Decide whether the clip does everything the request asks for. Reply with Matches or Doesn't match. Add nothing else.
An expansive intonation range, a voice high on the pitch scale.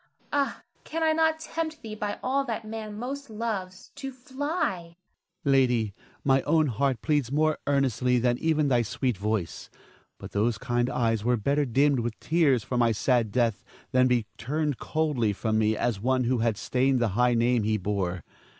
Doesn't match